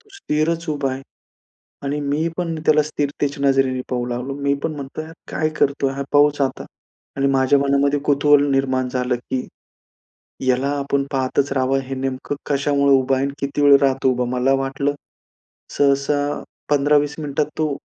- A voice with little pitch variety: Yes, narrow, 1.4 semitones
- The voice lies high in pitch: No, medium, 140 Hz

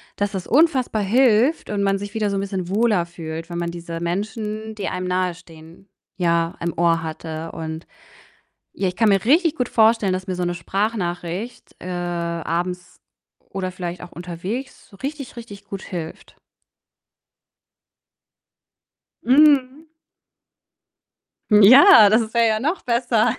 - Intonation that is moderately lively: Yes, average, 4.7 semitones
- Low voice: No, high, 195 Hz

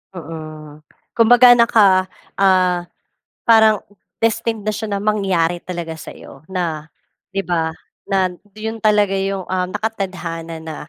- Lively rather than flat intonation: No, average, 4.3 semitones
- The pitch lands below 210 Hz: Yes, high, 190 Hz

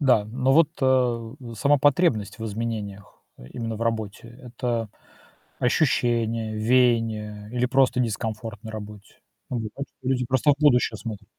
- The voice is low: Yes, low, 115 Hz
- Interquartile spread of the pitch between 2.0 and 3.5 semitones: Yes, average, 2.7 semitones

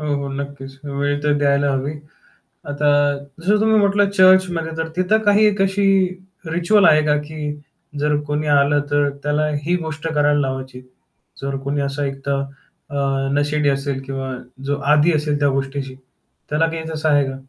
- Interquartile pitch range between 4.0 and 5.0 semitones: No, average, 2.7 semitones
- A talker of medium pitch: Yes, medium, 145 Hz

